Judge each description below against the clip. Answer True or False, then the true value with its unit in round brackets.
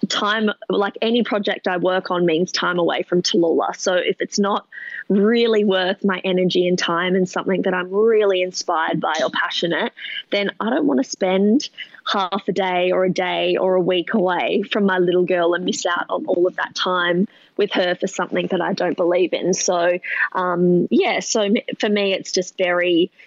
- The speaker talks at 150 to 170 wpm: False (200 wpm)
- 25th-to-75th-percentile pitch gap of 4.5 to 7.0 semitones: False (2.5 semitones)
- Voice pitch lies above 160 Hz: True (185 Hz)